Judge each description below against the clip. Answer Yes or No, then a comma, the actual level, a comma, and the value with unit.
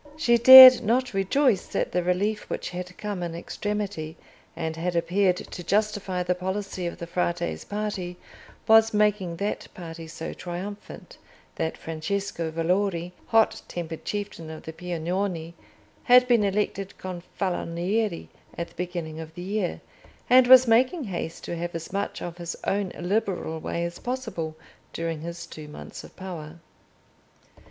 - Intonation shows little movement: No, average, 3.6 semitones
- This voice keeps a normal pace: Yes, average, 150 wpm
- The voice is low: No, medium, 180 Hz